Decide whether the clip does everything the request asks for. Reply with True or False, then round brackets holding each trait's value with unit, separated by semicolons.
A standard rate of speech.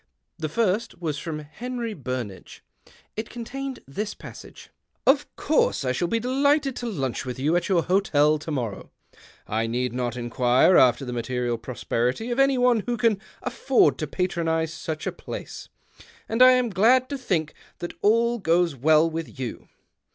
True (165 wpm)